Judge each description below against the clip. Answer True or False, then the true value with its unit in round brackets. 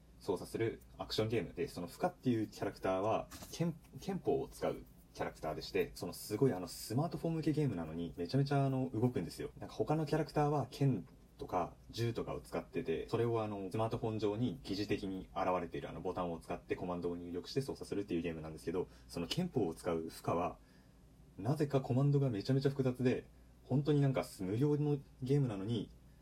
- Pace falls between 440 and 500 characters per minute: True (460 characters per minute)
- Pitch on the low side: True (120 Hz)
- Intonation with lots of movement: True (7.5 semitones)